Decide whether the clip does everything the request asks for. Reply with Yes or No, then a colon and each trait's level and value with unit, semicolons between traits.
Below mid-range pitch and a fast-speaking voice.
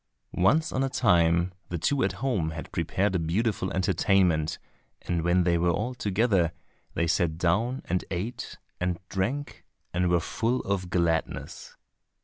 No: very low, 90 Hz; average, 150 wpm